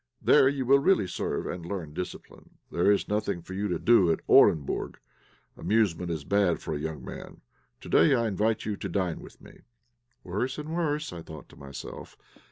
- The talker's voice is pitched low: Yes, low, 100 Hz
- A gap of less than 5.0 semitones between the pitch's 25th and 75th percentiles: No, wide, 5.6 semitones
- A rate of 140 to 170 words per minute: No, average, 190 wpm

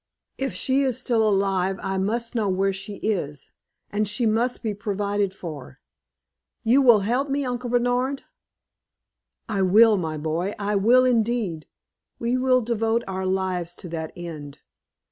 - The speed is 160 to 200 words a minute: No, average, 150 wpm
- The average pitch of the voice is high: Yes, high, 210 Hz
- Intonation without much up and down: No, average, 4.2 semitones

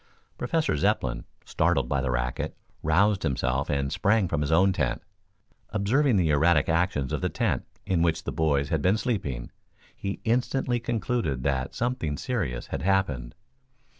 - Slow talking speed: No, average, 155 wpm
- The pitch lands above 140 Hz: No, very low, 85 Hz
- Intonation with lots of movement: Yes, wide, 7.5 semitones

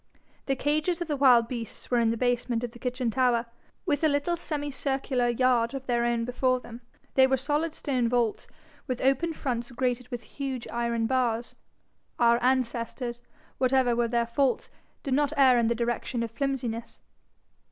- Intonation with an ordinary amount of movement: No, narrow, 2.3 semitones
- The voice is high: Yes, very high, 250 Hz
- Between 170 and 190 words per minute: Yes, average, 175 wpm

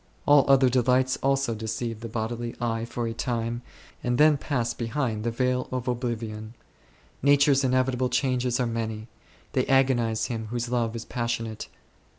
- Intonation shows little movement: Yes, narrow, 2.0 semitones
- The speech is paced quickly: No, average, 155 wpm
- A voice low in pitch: Yes, low, 120 Hz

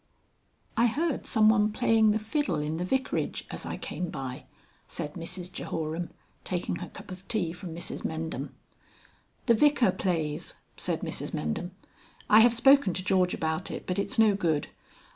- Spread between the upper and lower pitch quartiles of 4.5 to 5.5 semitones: Yes, average, 5.2 semitones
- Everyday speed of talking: Yes, average, 170 wpm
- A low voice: No, medium, 185 Hz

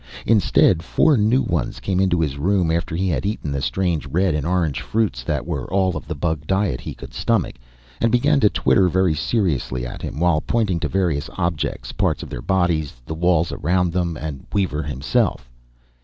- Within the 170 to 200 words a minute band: Yes, average, 195 wpm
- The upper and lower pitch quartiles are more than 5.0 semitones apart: No, average, 3.9 semitones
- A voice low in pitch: Yes, very low, 85 Hz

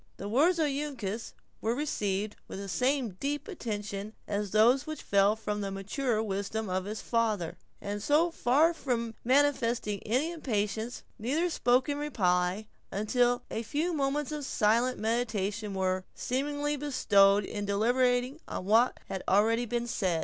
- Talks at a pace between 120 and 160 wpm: Yes, average, 150 wpm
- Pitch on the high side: Yes, high, 230 Hz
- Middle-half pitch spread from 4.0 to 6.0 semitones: Yes, average, 5.0 semitones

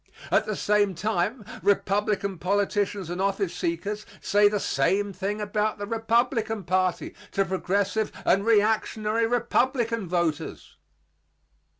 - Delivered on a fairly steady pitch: Yes, narrow, 2.2 semitones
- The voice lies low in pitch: No, high, 205 Hz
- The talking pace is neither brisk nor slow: No, slow, 115 wpm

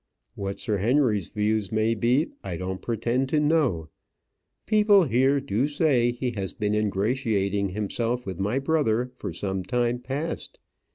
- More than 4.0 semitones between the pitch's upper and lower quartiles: Yes, average, 4.9 semitones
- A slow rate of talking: No, average, 155 wpm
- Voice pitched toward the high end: No, low, 115 Hz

